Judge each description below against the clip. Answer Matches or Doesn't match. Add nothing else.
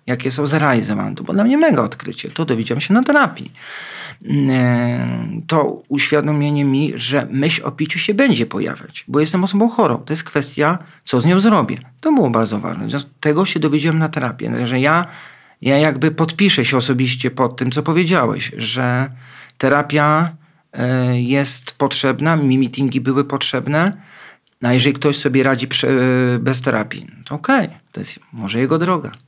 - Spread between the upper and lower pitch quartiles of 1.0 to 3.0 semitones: Doesn't match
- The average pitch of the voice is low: Doesn't match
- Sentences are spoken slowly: Doesn't match